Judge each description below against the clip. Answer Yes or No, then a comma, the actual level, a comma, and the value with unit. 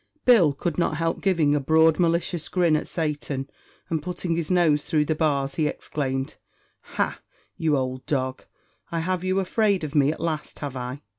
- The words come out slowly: No, average, 180 wpm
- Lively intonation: No, average, 3.1 semitones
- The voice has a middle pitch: Yes, medium, 155 Hz